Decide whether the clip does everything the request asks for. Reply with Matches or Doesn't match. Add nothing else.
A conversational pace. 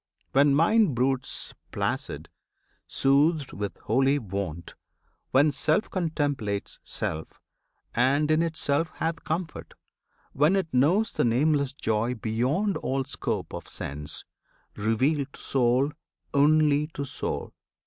Doesn't match